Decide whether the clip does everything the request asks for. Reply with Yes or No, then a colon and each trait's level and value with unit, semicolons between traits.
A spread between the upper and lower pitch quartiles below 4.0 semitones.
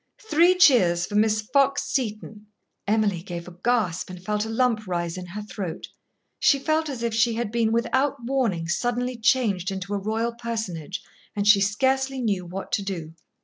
No: average, 4.5 semitones